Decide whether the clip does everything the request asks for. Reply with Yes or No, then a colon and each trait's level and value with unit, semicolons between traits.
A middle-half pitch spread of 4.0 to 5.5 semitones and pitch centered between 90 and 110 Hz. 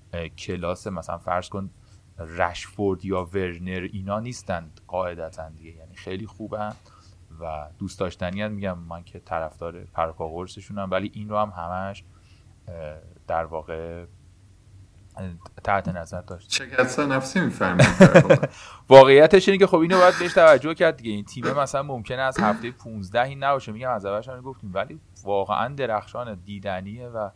No: average, 3.3 semitones; low, 100 Hz